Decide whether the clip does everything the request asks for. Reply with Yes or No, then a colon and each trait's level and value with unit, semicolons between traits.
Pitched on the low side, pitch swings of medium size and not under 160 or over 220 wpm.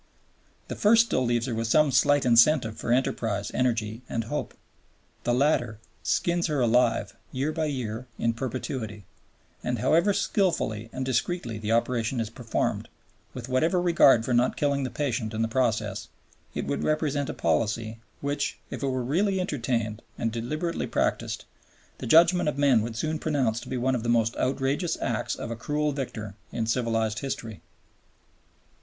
Yes: low, 125 Hz; average, 4.4 semitones; average, 165 wpm